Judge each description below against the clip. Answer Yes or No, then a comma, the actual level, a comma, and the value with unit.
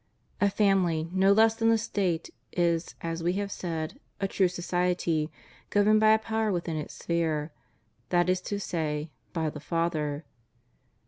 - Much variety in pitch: No, average, 3.6 semitones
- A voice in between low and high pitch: Yes, medium, 175 Hz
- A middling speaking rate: Yes, average, 155 wpm